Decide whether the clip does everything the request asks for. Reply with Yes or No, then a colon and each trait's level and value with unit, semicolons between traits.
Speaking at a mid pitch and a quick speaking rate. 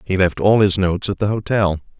No: very low, 95 Hz; fast, 240 wpm